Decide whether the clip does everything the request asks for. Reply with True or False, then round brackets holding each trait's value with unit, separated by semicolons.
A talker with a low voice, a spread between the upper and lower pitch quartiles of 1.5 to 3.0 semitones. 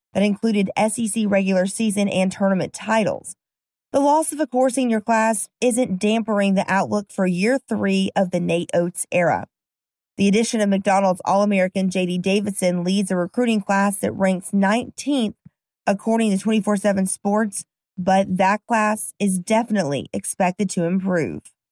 False (200 Hz; 2.7 semitones)